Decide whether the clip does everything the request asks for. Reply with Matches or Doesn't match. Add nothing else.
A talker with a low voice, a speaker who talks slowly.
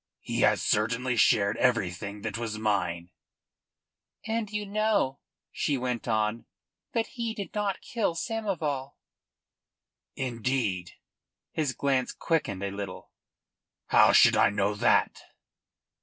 Matches